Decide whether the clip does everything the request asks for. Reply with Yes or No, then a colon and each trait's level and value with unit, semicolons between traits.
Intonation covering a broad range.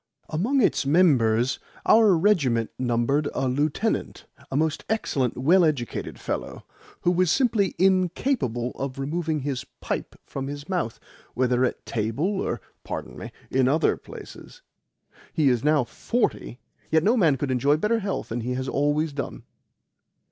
Yes: wide, 6.1 semitones